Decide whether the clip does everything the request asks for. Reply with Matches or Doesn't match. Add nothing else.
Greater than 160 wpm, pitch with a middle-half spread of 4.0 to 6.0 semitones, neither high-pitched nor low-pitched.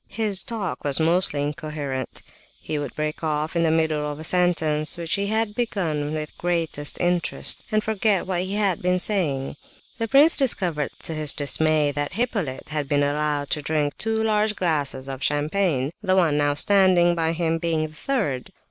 Matches